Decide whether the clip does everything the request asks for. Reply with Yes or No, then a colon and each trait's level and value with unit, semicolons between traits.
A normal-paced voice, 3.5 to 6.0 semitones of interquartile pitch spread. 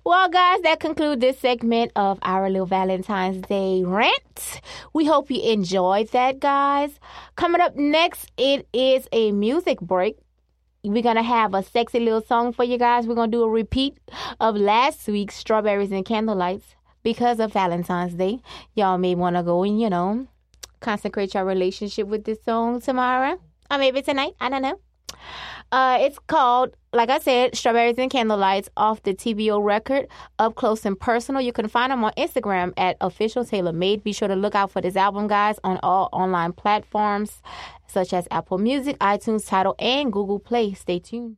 Yes: average, 180 wpm; average, 4.5 semitones